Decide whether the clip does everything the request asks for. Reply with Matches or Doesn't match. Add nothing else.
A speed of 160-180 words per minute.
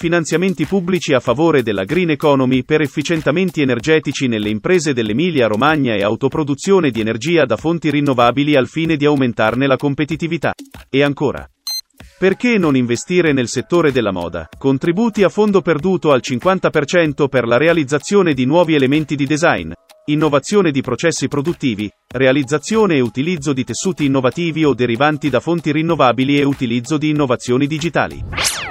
Doesn't match